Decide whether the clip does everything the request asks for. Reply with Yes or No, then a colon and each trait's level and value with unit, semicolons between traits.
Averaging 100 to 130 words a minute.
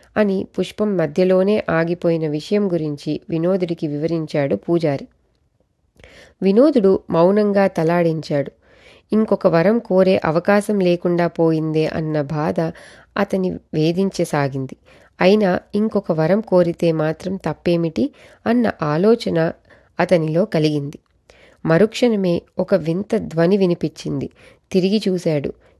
No: average, 90 wpm